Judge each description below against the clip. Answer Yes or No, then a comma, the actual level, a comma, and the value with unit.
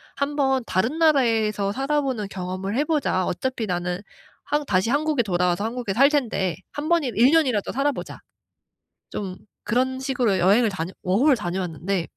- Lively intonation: Yes, wide, 6.5 semitones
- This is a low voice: No, high, 230 Hz